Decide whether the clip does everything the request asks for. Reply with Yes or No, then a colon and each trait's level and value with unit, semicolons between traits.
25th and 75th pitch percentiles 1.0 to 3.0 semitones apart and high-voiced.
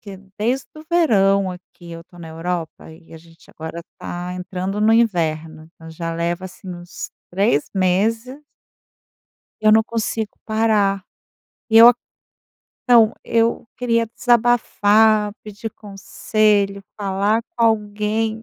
No: average, 3.9 semitones; high, 205 Hz